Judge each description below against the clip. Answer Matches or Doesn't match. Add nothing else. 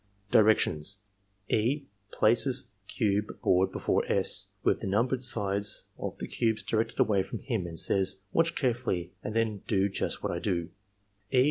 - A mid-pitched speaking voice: Doesn't match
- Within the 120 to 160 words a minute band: Doesn't match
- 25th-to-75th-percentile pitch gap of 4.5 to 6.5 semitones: Doesn't match